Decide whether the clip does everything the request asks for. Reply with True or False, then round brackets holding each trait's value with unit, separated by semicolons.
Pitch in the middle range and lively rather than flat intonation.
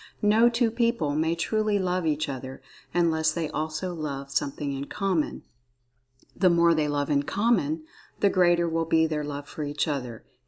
False (160 Hz; 3.9 semitones)